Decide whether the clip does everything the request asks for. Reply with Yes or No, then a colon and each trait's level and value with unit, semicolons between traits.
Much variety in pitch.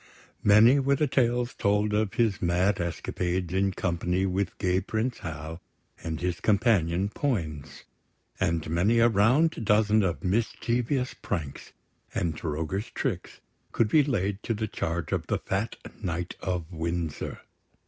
No: average, 4.7 semitones